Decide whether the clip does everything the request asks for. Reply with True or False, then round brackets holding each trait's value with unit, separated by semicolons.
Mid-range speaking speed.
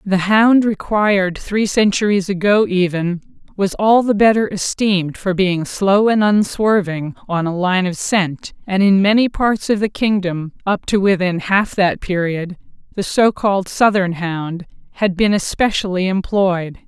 True (155 wpm)